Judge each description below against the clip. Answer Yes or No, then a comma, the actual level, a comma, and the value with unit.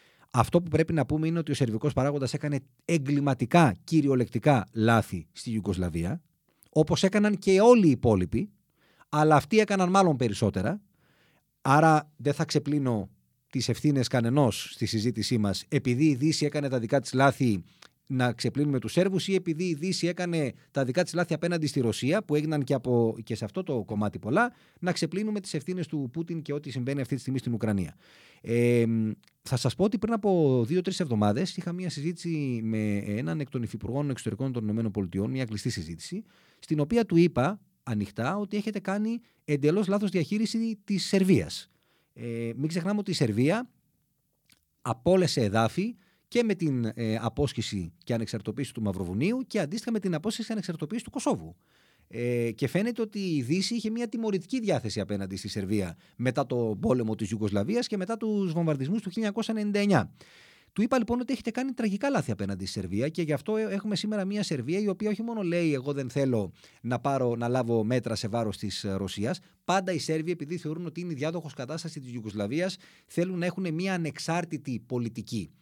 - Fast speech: Yes, fast, 175 wpm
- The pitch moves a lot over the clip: Yes, wide, 7.8 semitones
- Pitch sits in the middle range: Yes, medium, 150 Hz